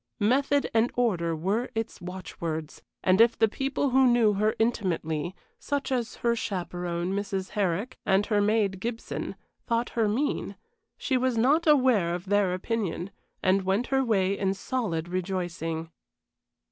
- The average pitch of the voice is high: Yes, high, 205 Hz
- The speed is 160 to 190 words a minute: No, average, 145 wpm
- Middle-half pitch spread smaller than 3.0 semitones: No, average, 4.6 semitones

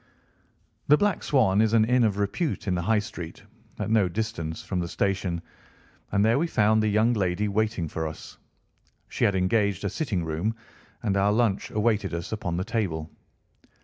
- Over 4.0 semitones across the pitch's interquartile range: No, average, 3.6 semitones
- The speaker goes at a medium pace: Yes, average, 180 wpm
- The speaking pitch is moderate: No, low, 100 Hz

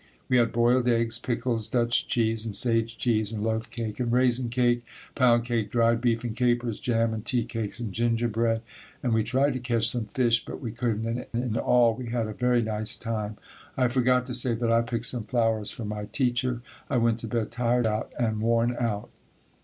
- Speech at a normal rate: No, fast, 210 wpm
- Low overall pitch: Yes, low, 115 Hz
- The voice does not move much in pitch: Yes, narrow, 1.4 semitones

